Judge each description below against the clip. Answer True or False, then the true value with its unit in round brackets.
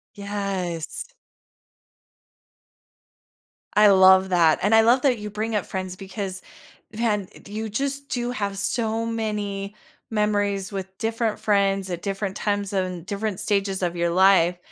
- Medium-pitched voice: False (200 Hz)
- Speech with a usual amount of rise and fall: False (2.2 semitones)